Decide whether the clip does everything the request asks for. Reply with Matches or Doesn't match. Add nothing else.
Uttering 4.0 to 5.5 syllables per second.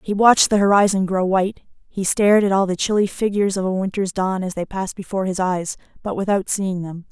Doesn't match